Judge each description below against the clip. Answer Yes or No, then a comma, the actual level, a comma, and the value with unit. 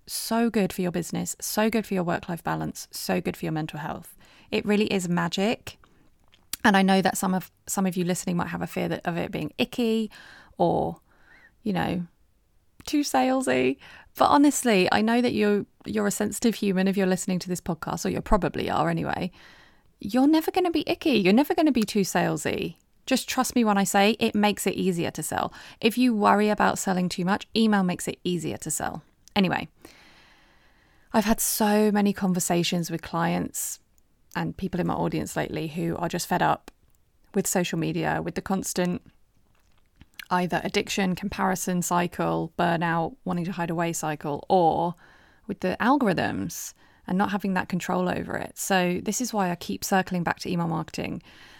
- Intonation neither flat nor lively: Yes, average, 3.5 semitones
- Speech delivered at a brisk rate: No, average, 185 wpm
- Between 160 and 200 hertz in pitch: Yes, high, 190 Hz